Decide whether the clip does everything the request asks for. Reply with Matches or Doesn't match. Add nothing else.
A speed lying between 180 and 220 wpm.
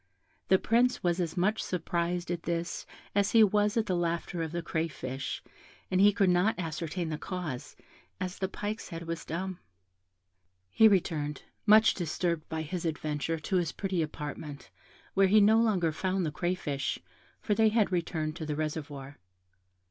Doesn't match